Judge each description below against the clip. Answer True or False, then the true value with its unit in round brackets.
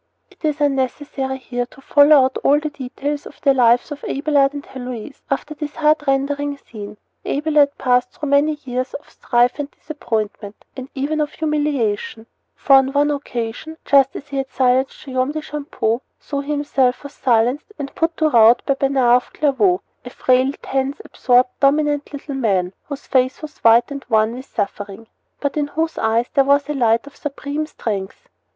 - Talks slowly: False (180 wpm)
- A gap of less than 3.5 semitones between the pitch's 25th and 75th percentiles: True (2.8 semitones)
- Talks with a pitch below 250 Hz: False (275 Hz)